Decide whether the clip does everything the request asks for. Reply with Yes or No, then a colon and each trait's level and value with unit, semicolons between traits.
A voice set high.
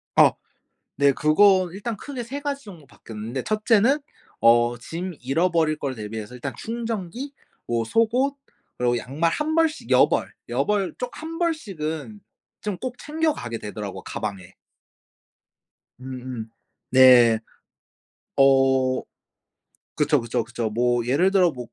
No: medium, 155 Hz